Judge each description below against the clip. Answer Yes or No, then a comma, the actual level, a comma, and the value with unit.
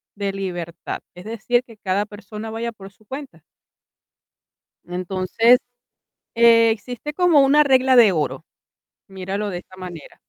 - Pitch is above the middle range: Yes, high, 210 Hz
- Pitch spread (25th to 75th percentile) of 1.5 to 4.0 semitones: No, average, 4.4 semitones